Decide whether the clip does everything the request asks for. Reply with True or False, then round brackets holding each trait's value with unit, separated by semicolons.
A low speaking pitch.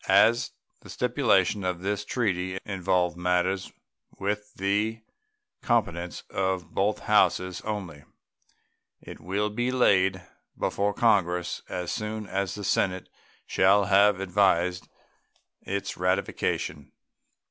True (95 Hz)